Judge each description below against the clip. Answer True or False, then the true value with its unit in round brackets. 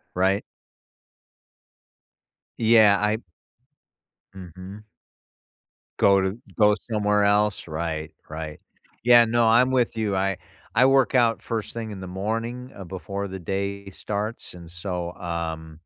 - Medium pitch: False (100 Hz)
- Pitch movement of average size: True (3.4 semitones)